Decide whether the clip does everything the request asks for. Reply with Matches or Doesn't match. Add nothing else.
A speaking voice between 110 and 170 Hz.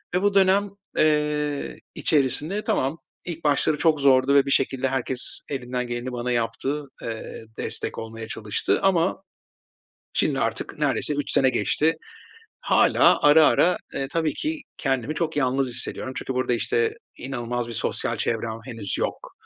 Matches